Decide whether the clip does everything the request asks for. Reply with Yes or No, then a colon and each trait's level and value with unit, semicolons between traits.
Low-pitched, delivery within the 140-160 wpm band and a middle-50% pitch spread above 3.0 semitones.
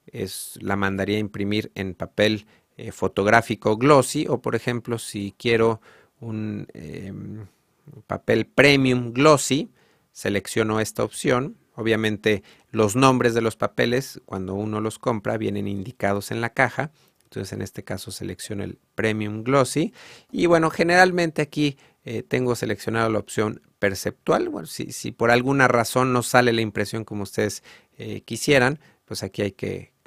Yes: low, 115 Hz; average, 150 wpm; average, 3.5 semitones